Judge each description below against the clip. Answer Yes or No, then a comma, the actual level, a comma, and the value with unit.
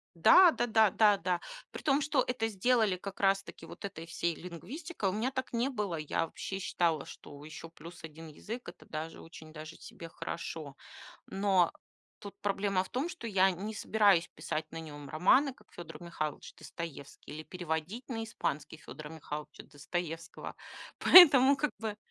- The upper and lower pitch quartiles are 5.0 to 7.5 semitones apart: Yes, wide, 5.5 semitones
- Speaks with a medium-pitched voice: Yes, medium, 180 Hz